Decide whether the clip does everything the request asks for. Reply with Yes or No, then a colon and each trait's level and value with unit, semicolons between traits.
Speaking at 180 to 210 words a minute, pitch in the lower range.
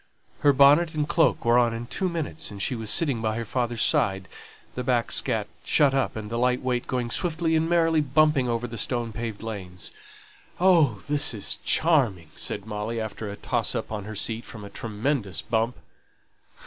Yes: average, 190 wpm; low, 120 Hz